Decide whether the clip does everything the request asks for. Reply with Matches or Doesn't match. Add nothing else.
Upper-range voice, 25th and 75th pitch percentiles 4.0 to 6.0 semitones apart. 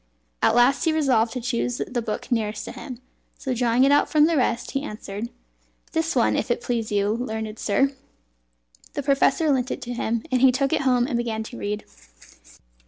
Doesn't match